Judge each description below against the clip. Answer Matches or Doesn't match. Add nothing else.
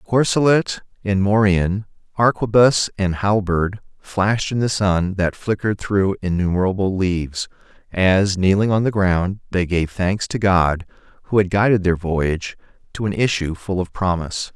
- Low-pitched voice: Matches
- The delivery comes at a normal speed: Matches